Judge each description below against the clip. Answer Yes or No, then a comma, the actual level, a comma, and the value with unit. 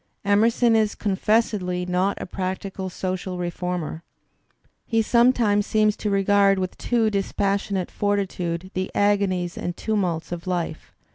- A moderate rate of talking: No, slow, 130 wpm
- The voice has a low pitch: No, high, 195 Hz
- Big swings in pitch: No, narrow, 2.5 semitones